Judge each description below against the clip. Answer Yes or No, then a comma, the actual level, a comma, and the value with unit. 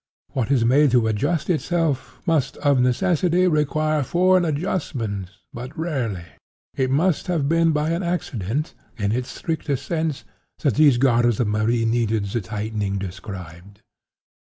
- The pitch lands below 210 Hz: Yes, low, 135 Hz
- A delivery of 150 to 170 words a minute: No, average, 140 wpm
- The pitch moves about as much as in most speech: No, wide, 6.3 semitones